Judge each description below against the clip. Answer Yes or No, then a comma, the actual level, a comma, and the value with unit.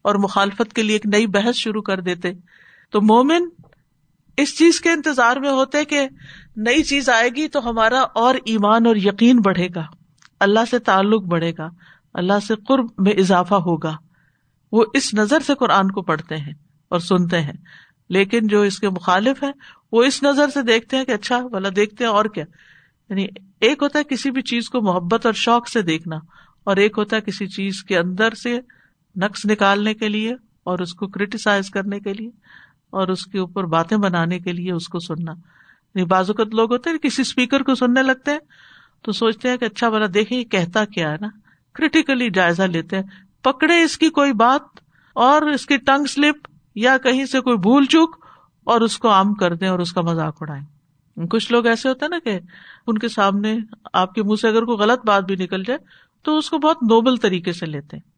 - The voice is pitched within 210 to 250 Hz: Yes, high, 215 Hz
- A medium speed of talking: No, fast, 205 wpm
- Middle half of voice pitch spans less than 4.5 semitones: No, average, 5.1 semitones